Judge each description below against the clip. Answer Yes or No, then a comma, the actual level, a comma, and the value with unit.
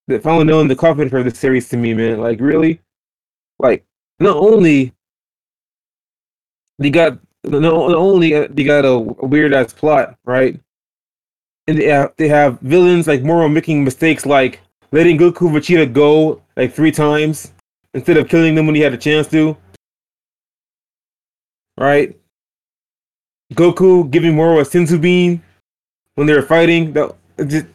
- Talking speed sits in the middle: Yes, average, 150 wpm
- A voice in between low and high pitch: Yes, medium, 150 Hz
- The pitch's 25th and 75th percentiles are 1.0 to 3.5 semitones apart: Yes, average, 2.9 semitones